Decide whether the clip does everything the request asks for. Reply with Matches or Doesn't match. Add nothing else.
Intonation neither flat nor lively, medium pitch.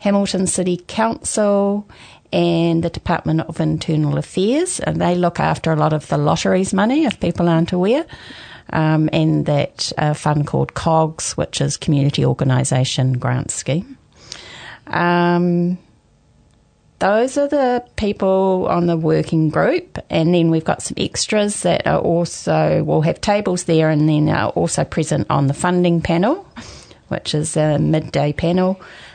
Matches